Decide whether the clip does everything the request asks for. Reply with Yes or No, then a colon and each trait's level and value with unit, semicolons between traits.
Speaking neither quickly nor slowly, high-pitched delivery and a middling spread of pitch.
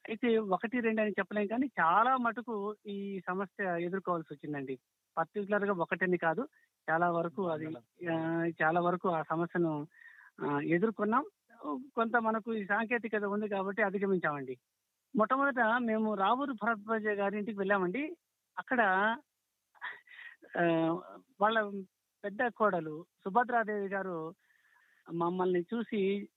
Yes: average, 100 wpm; high, 200 Hz; average, 4.8 semitones